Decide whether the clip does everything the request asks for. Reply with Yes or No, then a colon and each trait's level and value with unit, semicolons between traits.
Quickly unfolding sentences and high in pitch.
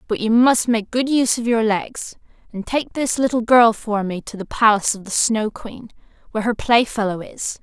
Yes: fast, 210 wpm; high, 225 Hz